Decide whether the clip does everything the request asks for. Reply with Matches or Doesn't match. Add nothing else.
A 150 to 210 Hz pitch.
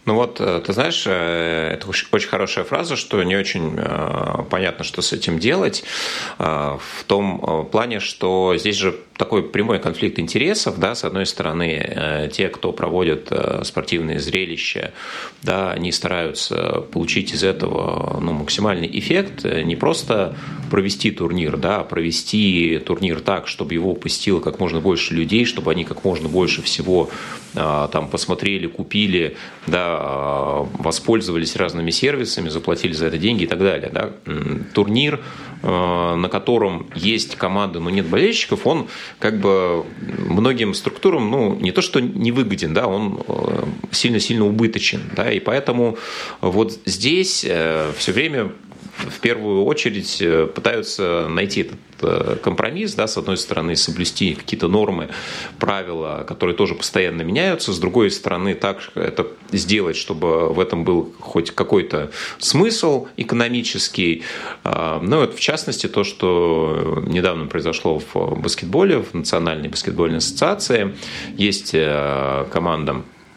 Doesn't match